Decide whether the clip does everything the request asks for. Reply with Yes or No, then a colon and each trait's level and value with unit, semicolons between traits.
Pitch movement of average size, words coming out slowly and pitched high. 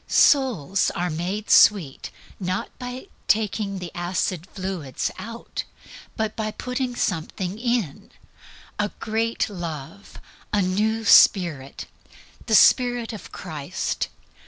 Yes: average, 4.2 semitones; slow, 110 wpm; high, 200 Hz